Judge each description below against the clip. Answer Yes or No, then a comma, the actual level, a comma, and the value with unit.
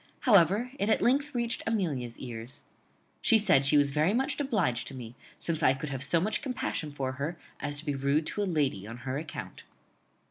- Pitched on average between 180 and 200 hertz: No, medium, 150 Hz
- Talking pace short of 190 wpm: No, fast, 205 wpm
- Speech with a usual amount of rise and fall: No, wide, 7.5 semitones